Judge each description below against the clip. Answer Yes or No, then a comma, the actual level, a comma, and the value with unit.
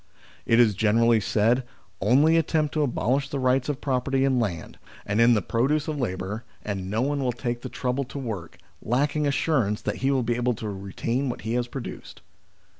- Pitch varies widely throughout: No, average, 3.8 semitones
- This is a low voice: Yes, low, 120 Hz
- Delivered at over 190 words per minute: Yes, average, 200 wpm